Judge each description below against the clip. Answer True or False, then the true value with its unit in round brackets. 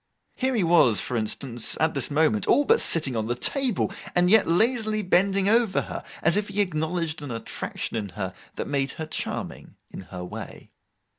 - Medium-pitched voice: True (165 Hz)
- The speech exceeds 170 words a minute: True (180 wpm)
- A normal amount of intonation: False (8.9 semitones)